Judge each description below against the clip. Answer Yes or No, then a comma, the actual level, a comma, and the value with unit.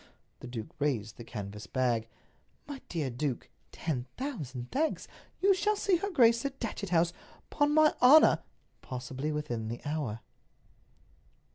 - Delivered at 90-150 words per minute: Yes, average, 140 wpm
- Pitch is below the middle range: No, medium, 150 Hz